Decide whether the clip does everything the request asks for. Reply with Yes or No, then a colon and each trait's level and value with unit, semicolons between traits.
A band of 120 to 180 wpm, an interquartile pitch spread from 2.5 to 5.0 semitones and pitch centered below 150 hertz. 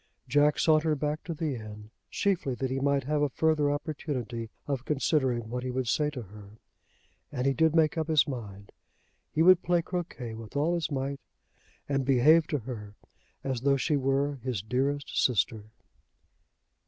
Yes: average, 170 wpm; average, 3.7 semitones; low, 135 Hz